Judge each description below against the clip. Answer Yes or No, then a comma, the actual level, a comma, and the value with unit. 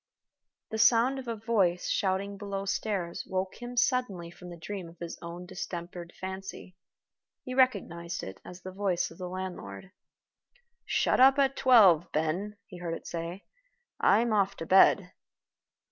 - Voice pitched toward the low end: No, high, 190 Hz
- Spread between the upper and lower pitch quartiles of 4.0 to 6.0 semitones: No, average, 3.5 semitones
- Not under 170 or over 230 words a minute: No, average, 155 wpm